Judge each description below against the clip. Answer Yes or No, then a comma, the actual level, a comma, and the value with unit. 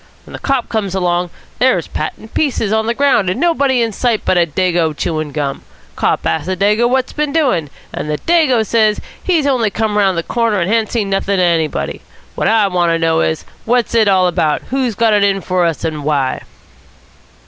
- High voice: Yes, high, 200 Hz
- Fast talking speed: Yes, fast, 215 wpm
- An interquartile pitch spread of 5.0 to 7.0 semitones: Yes, wide, 5.4 semitones